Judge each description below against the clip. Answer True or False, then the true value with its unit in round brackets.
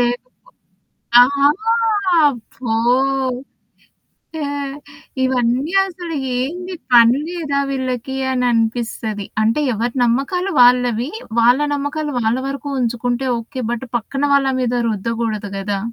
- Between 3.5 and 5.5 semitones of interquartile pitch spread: False (2.9 semitones)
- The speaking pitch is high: True (245 Hz)